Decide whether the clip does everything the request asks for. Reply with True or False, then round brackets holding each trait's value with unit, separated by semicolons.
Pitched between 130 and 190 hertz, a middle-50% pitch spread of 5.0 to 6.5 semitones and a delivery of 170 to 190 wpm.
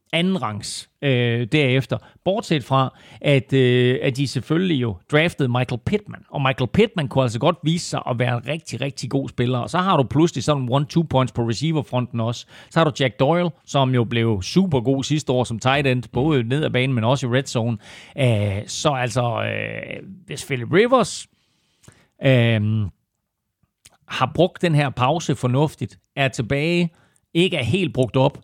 False (135 Hz; 3.5 semitones; 185 wpm)